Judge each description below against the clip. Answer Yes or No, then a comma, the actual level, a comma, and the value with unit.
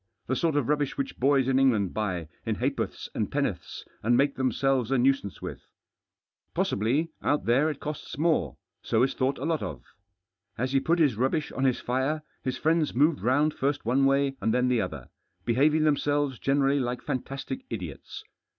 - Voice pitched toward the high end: No, low, 135 Hz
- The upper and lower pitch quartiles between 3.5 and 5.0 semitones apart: No, average, 3.0 semitones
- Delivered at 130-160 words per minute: No, average, 180 wpm